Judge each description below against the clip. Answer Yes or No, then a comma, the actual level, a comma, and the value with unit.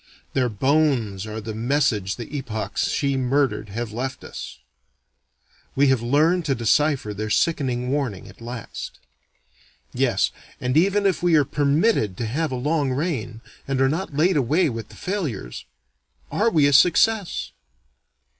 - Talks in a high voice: No, low, 135 Hz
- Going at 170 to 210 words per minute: No, average, 150 wpm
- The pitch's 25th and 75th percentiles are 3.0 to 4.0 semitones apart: No, average, 5.1 semitones